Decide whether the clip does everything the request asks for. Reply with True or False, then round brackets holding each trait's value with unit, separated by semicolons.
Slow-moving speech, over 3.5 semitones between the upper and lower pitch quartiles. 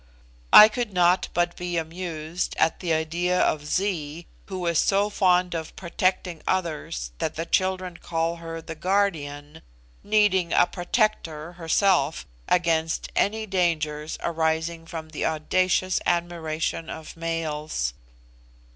False (120 wpm; 2.5 semitones)